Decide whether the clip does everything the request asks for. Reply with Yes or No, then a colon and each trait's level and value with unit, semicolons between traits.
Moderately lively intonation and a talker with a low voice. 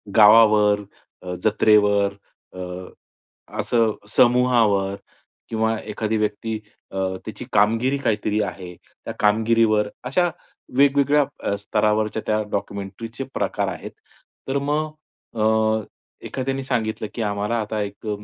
No: narrow, 2.1 semitones; low, 110 Hz